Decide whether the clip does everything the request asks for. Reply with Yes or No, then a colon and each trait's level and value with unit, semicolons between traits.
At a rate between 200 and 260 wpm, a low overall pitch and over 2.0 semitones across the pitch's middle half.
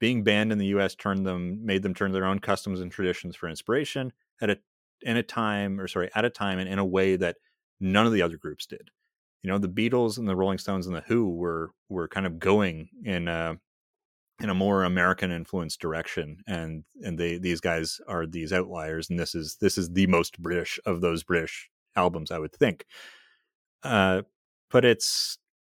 Yes: fast, 205 wpm; very low, 95 Hz; narrow, 2.5 semitones